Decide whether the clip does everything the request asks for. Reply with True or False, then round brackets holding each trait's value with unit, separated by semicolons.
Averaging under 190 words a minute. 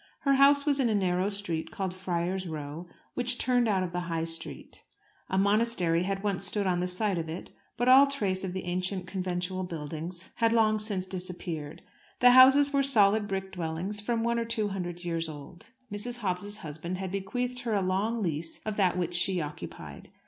False (195 wpm)